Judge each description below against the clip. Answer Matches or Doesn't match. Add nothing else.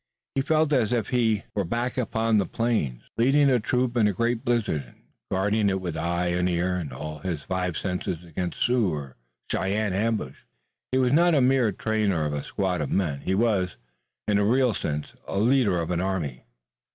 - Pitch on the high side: Doesn't match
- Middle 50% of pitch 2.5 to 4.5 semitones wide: Doesn't match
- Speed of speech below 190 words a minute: Doesn't match